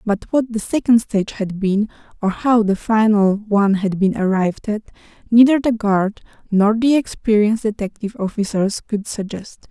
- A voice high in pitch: Yes, high, 210 Hz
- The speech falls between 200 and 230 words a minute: No, average, 160 wpm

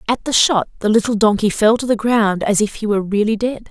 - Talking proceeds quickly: Yes, fast, 260 wpm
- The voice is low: No, high, 215 Hz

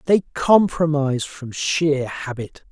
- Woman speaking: No, male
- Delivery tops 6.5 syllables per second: No, 3.6 syllables/s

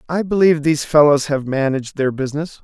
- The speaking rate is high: No, average, 180 wpm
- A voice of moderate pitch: Yes, medium, 145 Hz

